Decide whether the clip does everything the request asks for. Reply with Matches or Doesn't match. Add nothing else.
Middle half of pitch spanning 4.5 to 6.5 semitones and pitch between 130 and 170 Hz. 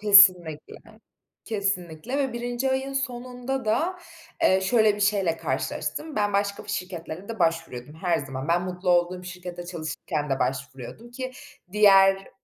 Doesn't match